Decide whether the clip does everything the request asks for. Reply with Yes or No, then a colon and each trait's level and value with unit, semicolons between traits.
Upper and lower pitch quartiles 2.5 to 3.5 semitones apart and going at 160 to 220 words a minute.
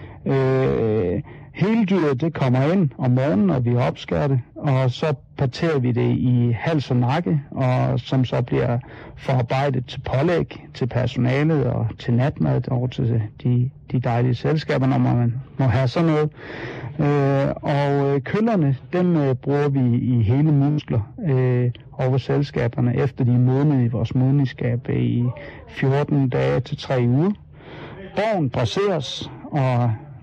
No: average, 3.0 semitones; slow, 145 wpm